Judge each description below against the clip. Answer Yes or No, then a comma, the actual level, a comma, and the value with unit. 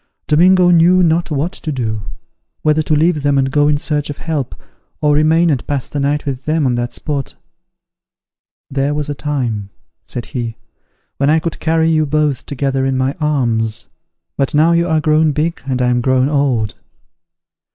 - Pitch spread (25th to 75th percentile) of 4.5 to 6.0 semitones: No, average, 3.0 semitones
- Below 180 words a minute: No, average, 185 wpm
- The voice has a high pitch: No, medium, 145 Hz